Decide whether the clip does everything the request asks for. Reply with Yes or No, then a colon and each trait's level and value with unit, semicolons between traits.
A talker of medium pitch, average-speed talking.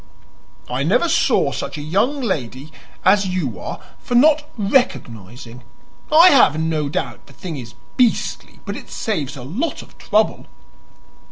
Yes: medium, 165 Hz; average, 150 wpm